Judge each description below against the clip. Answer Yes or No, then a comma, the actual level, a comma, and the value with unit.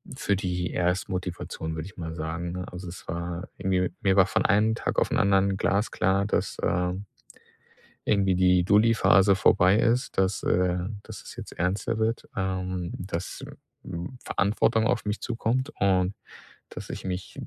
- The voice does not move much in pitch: Yes, narrow, 2.2 semitones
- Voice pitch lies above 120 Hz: No, very low, 95 Hz